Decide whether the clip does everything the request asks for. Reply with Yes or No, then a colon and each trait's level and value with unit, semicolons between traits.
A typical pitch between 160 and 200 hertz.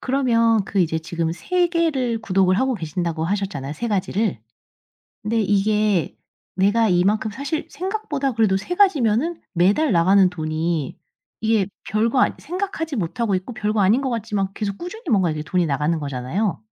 No: high, 210 Hz